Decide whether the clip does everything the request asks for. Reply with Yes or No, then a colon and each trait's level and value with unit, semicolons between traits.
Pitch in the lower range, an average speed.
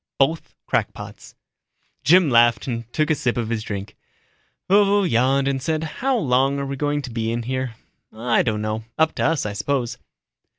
Yes: low, 130 Hz; average, 180 wpm